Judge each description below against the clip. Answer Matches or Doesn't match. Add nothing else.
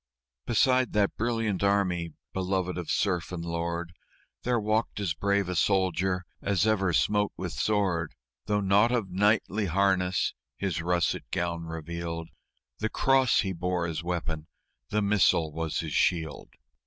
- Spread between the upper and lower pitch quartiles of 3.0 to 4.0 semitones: Matches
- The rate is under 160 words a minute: Matches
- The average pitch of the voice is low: Matches